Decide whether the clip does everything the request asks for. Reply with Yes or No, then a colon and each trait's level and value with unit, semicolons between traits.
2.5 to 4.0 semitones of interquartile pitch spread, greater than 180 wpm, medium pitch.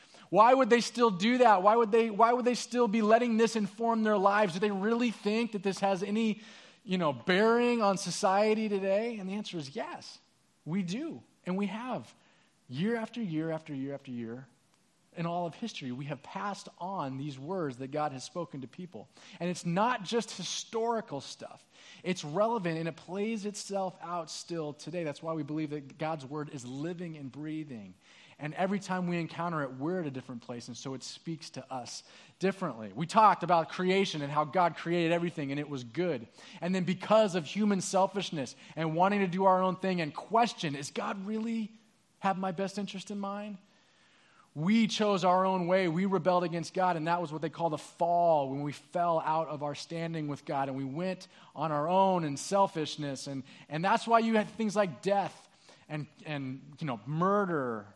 No: average, 5.1 semitones; average, 200 wpm; medium, 180 Hz